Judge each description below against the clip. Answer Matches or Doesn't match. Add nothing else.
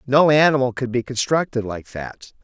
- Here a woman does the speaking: Doesn't match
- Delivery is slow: Doesn't match